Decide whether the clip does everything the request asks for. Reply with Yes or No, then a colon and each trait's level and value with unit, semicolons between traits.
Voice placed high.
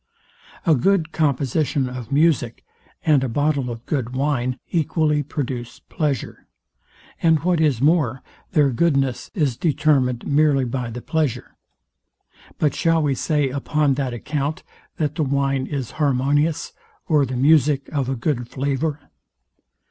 No: medium, 140 Hz